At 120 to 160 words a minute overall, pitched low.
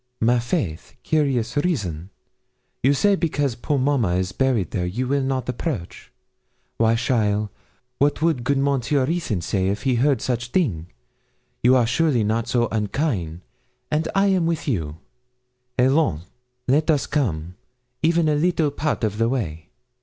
Yes: average, 155 wpm; low, 125 Hz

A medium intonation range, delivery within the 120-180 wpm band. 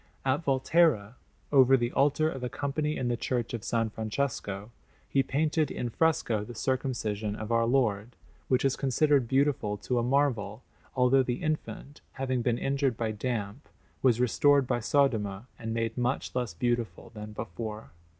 Yes: average, 3.6 semitones; average, 160 wpm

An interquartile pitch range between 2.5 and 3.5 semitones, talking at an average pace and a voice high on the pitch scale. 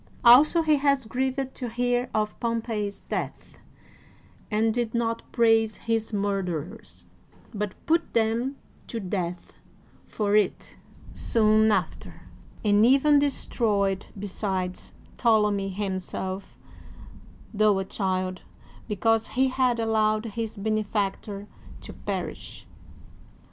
No: average, 2.8 semitones; slow, 105 wpm; high, 220 Hz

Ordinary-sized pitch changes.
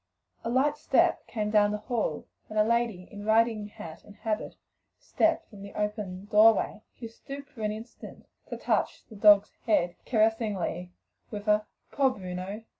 No: narrow, 1.8 semitones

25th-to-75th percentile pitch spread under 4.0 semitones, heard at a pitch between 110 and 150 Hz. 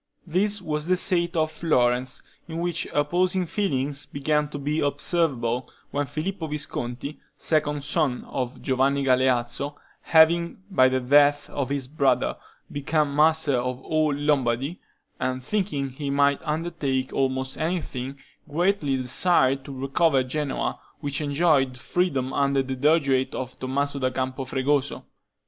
Yes: average, 3.2 semitones; medium, 140 Hz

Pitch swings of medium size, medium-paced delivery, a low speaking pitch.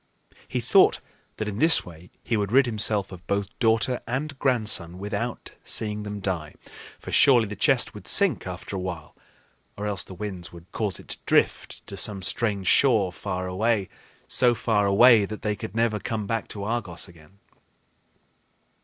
Yes: average, 3.6 semitones; average, 170 wpm; low, 105 Hz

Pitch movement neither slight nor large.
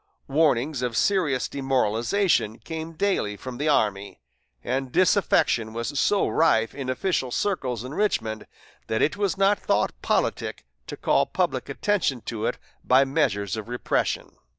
No: wide, 6.2 semitones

